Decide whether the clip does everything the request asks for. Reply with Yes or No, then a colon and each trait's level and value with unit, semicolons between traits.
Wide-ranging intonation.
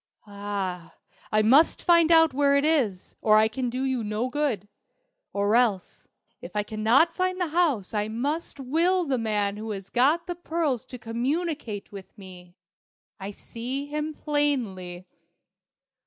Yes: wide, 6.5 semitones